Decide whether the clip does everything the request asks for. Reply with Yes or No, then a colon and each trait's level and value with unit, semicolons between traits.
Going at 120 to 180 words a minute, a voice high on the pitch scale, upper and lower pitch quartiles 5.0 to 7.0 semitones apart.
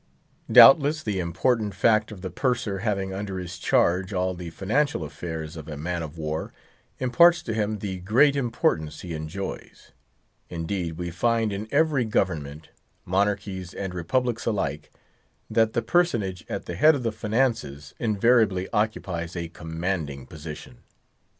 No: average, 140 wpm; very low, 95 Hz; average, 5.3 semitones